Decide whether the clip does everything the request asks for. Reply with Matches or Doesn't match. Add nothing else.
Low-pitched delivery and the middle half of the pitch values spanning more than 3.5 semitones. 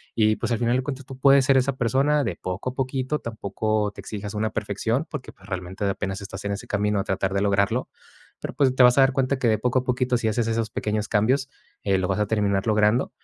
Matches